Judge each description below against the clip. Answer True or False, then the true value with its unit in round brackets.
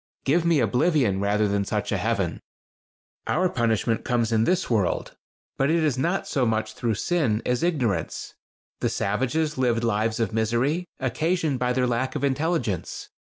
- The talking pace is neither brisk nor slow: True (160 wpm)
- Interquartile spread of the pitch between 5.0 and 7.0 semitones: True (5.5 semitones)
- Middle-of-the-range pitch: False (125 Hz)